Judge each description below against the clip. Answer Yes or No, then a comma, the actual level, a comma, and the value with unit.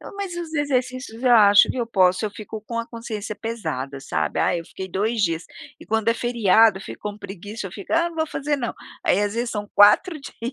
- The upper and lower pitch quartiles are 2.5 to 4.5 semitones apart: Yes, average, 3.5 semitones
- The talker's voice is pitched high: Yes, high, 225 Hz